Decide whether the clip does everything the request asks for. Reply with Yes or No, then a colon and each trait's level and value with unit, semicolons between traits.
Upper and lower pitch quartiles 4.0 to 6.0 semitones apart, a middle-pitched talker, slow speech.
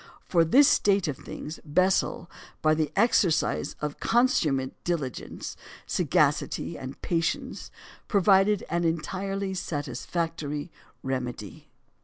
Yes: average, 4.8 semitones; medium, 165 Hz; slow, 100 wpm